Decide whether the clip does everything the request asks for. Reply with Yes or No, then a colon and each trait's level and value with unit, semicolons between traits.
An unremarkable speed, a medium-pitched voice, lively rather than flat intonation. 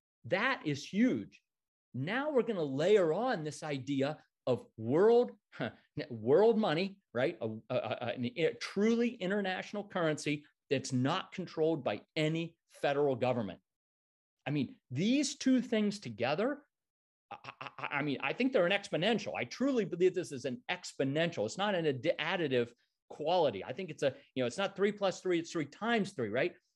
Yes: average, 165 wpm; medium, 165 Hz; wide, 7.1 semitones